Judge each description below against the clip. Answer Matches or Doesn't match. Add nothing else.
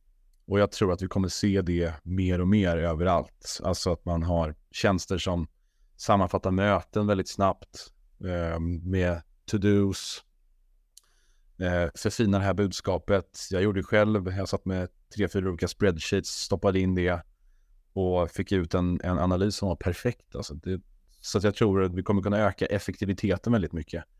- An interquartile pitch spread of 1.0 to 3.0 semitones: Matches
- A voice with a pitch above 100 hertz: Doesn't match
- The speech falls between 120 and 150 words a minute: Doesn't match